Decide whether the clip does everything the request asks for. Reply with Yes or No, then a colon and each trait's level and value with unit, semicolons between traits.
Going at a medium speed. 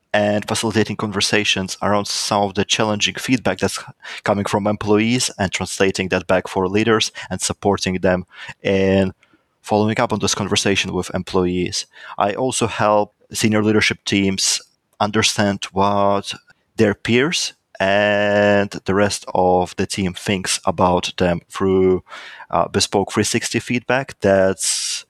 No: slow, 130 wpm